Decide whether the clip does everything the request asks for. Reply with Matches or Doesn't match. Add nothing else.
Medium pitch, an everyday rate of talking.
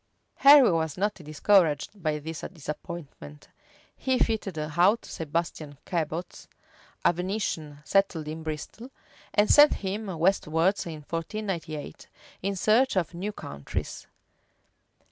Doesn't match